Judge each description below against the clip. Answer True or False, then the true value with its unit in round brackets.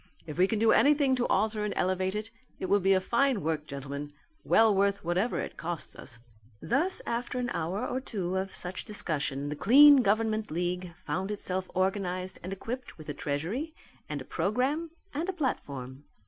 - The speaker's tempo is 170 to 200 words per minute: True (185 wpm)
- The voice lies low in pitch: False (195 Hz)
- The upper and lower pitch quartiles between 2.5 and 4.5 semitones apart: False (5.4 semitones)